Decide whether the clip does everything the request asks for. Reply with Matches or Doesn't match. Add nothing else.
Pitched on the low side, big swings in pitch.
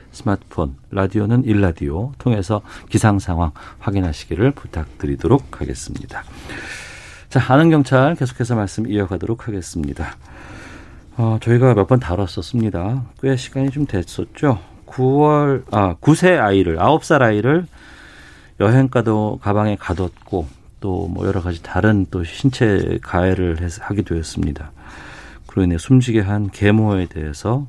Matches